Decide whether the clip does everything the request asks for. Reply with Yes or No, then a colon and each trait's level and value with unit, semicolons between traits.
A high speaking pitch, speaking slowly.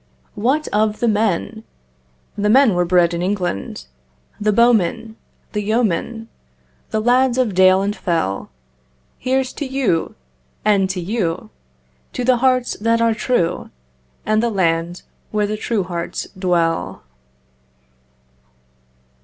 Yes: high, 210 Hz; slow, 120 wpm